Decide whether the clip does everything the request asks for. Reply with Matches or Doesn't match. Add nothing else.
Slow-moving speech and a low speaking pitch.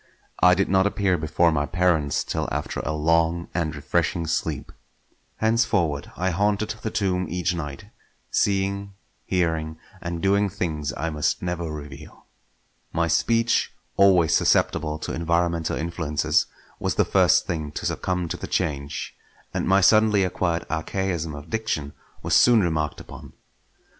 Doesn't match